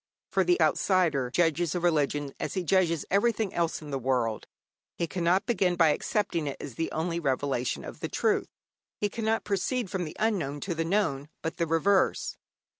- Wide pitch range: No, average, 4.7 semitones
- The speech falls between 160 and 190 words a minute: Yes, average, 180 wpm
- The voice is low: No, medium, 170 Hz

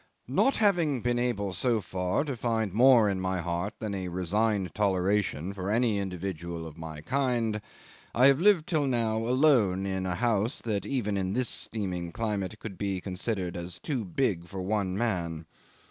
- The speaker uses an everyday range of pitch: Yes, average, 4.5 semitones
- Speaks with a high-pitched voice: No, low, 100 Hz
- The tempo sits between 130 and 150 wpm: No, average, 175 wpm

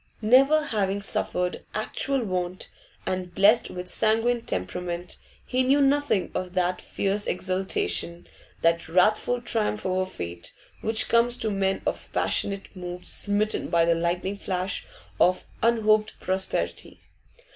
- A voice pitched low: No, high, 195 Hz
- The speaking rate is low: Yes, slow, 125 wpm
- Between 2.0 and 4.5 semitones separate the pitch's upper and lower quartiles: Yes, average, 3.6 semitones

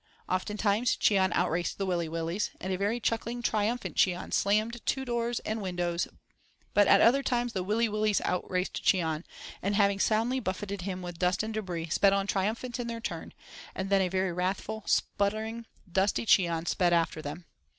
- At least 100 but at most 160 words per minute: No, average, 175 wpm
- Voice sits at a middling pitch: No, high, 200 Hz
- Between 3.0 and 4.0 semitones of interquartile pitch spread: Yes, average, 3.5 semitones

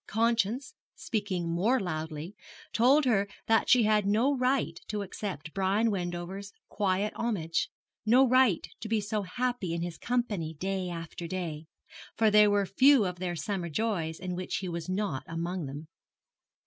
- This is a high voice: Yes, high, 195 Hz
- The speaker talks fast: No, average, 160 wpm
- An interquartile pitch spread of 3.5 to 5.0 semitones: Yes, average, 4.4 semitones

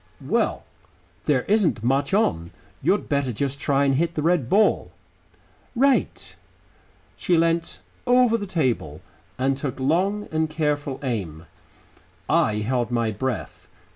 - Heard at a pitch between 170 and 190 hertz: No, medium, 140 Hz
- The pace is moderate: No, slow, 130 wpm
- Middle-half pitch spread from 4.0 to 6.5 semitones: Yes, wide, 5.5 semitones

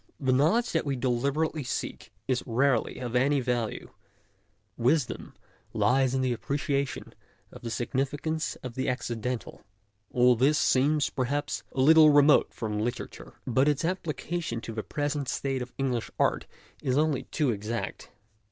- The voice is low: Yes, low, 130 Hz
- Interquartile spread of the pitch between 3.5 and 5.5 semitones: No, average, 3.1 semitones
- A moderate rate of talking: Yes, average, 145 wpm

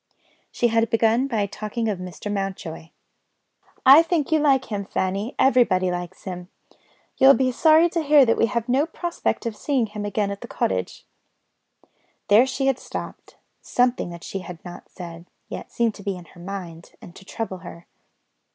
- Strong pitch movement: Yes, wide, 5.9 semitones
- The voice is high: Yes, high, 210 Hz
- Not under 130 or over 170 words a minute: No, average, 180 wpm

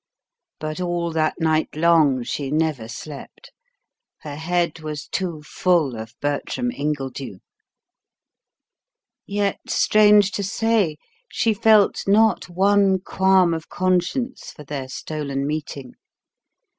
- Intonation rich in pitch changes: No, average, 4.6 semitones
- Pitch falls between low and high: Yes, medium, 165 Hz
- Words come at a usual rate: No, slow, 110 wpm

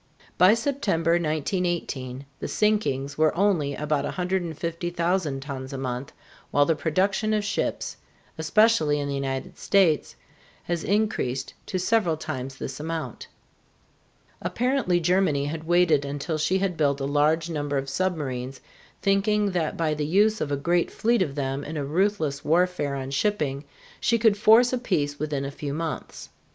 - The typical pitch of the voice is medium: Yes, medium, 160 Hz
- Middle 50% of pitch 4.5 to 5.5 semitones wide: Yes, average, 5.1 semitones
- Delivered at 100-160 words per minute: Yes, average, 155 wpm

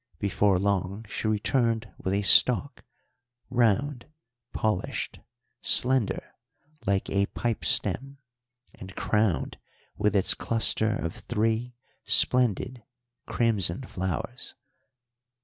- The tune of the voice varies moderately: Yes, average, 3.4 semitones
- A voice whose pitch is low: Yes, low, 110 Hz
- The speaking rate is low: Yes, slow, 95 wpm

